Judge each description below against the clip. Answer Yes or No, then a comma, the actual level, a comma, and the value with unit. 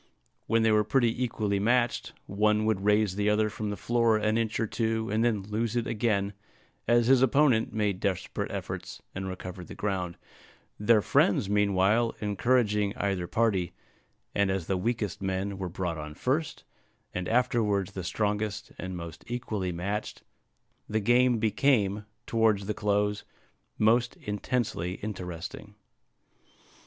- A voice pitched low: Yes, low, 105 Hz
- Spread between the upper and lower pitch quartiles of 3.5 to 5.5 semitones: No, average, 2.8 semitones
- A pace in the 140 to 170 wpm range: Yes, average, 145 wpm